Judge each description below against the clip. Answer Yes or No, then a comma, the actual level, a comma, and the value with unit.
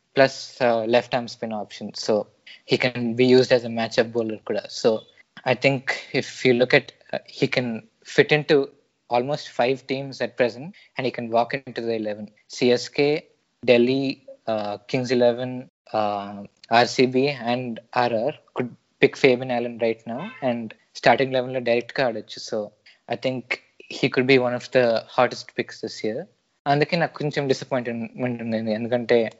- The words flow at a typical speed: No, fast, 160 wpm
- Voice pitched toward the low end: Yes, low, 125 Hz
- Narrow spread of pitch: Yes, narrow, 2.3 semitones